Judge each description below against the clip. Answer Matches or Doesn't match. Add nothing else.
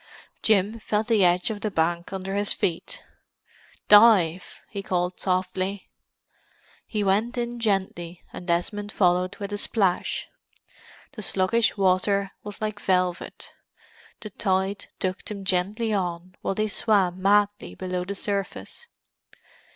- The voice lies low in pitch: Doesn't match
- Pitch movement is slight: Matches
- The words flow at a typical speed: Doesn't match